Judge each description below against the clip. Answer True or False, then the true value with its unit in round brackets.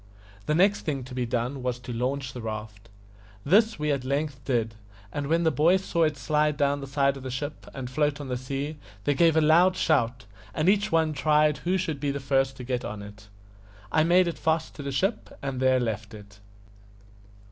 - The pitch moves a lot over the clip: False (3.7 semitones)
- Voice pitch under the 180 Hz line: True (140 Hz)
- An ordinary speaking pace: False (215 wpm)